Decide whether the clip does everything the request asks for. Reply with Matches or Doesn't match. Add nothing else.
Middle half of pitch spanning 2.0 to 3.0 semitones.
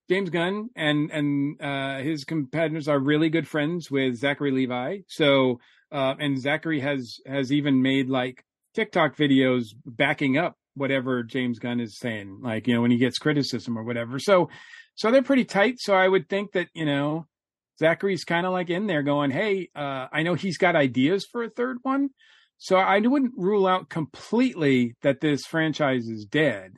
Doesn't match